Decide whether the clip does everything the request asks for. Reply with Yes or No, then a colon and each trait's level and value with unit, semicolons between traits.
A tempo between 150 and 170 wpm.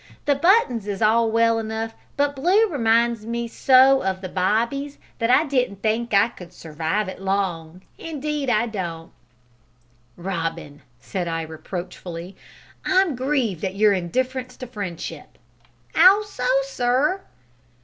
No: slow, 135 wpm